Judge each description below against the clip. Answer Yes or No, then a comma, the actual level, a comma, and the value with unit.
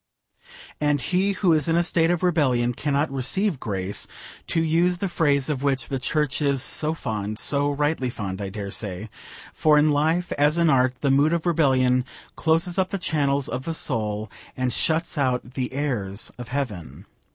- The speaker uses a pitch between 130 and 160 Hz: Yes, medium, 140 Hz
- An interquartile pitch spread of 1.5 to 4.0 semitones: No, average, 4.5 semitones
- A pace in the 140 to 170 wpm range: No, average, 185 wpm